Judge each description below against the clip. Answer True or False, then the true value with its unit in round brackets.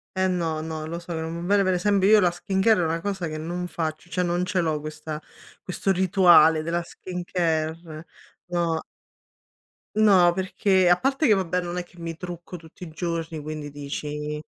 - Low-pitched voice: False (175 Hz)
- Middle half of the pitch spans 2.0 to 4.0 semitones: True (2.4 semitones)